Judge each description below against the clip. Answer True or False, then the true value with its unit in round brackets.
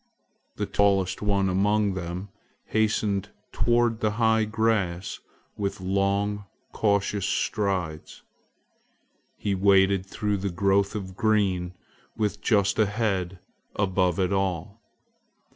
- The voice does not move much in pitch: True (1.9 semitones)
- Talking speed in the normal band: False (110 wpm)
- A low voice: True (100 Hz)